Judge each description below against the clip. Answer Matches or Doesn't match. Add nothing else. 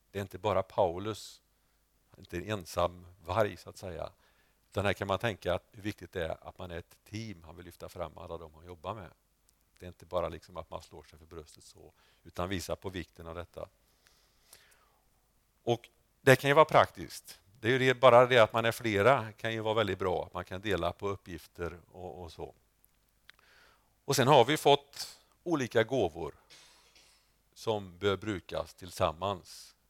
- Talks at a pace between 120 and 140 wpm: Doesn't match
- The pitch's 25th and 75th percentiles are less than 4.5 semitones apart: Matches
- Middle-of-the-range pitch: Doesn't match